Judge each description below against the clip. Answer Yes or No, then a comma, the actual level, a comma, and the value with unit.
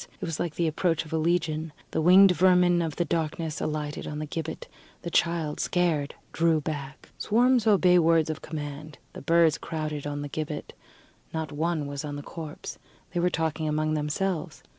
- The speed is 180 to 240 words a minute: Yes, average, 185 wpm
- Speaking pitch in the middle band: Yes, medium, 160 Hz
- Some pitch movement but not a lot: No, narrow, 2.3 semitones